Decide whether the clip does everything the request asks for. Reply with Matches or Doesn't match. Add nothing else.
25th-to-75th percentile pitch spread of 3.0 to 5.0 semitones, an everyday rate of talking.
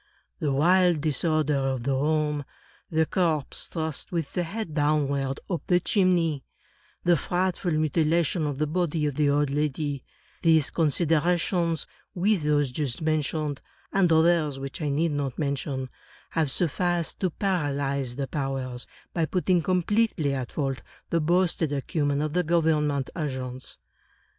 Matches